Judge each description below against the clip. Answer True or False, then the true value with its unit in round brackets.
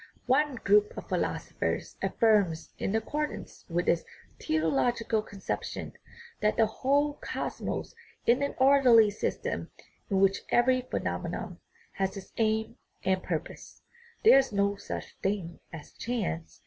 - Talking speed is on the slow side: True (125 wpm)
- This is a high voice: True (220 Hz)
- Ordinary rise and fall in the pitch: True (5.0 semitones)